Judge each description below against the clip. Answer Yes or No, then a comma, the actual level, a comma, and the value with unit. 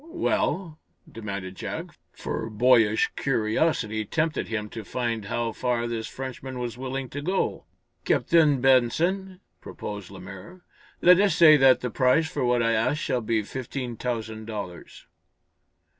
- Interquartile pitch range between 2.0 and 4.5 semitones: No, average, 4.9 semitones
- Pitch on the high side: No, low, 125 Hz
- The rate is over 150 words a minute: No, average, 140 wpm